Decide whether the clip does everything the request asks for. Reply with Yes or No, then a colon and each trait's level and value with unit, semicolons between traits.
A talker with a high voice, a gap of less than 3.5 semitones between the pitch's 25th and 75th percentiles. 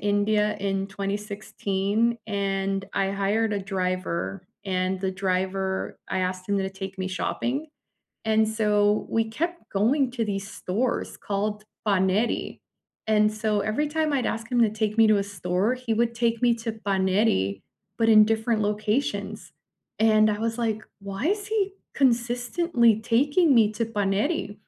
Yes: high, 210 Hz; average, 2.9 semitones